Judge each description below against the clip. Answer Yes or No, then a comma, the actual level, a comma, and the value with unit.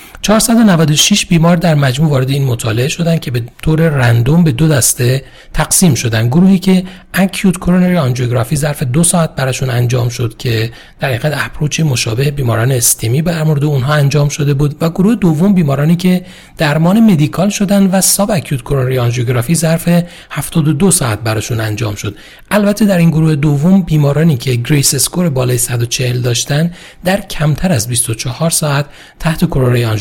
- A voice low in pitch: No, medium, 150 Hz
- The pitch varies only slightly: No, average, 5.3 semitones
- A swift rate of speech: Yes, fast, 160 wpm